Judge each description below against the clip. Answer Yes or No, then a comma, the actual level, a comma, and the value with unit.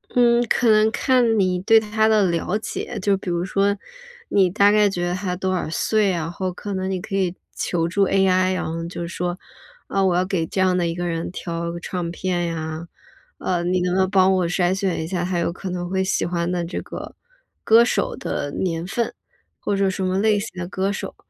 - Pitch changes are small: Yes, narrow, 2.3 semitones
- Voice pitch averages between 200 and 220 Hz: No, medium, 185 Hz